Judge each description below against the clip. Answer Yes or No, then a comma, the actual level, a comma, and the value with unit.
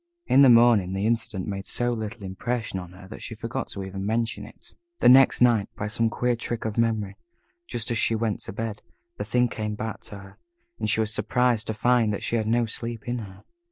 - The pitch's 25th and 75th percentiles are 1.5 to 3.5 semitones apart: Yes, narrow, 2.6 semitones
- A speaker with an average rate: No, fast, 230 wpm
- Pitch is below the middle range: Yes, low, 110 Hz